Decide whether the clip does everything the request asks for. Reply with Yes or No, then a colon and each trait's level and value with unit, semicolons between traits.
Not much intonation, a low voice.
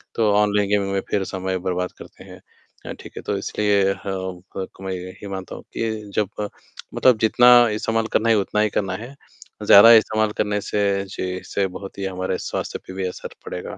Yes: narrow, 2.1 semitones; low, 100 Hz